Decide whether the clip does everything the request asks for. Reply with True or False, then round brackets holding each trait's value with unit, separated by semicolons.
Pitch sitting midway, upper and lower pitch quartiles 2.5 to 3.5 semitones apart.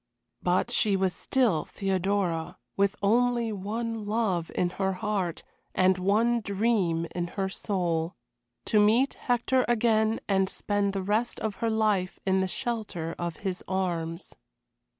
False (200 Hz; 3.2 semitones)